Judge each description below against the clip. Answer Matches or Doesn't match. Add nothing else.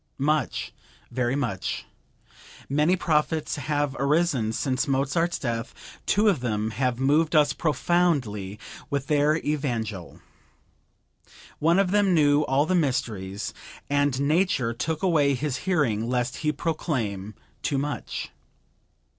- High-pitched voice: Doesn't match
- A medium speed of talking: Doesn't match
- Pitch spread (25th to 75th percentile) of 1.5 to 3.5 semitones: Doesn't match